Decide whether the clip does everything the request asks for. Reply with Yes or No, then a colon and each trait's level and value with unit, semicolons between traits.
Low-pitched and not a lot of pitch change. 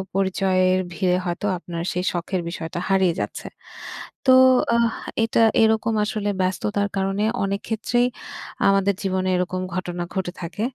No: high, 190 Hz; narrow, 2.3 semitones